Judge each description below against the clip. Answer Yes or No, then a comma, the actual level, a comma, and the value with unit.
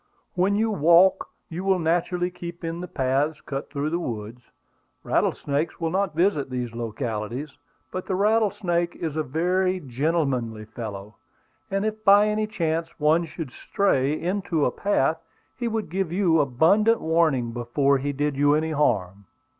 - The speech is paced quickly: No, average, 155 wpm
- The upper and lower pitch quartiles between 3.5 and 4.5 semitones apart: No, wide, 5.4 semitones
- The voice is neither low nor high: Yes, medium, 160 Hz